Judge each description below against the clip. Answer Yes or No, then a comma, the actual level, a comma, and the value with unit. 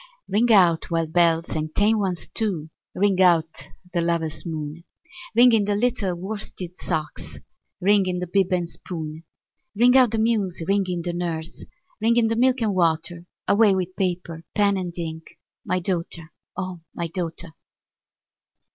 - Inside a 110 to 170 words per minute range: Yes, average, 160 wpm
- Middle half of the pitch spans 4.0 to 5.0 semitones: No, average, 3.5 semitones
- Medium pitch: Yes, medium, 180 Hz